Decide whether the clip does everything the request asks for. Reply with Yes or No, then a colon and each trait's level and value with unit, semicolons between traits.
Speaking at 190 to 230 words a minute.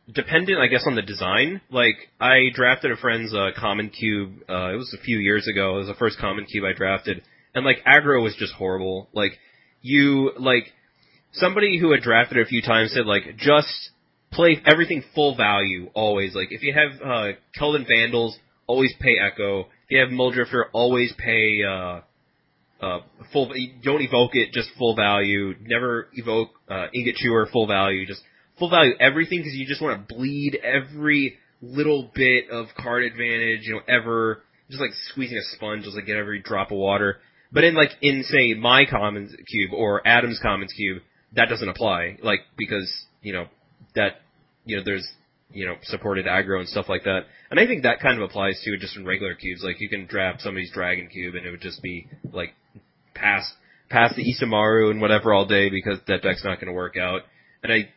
Yes: average, 200 wpm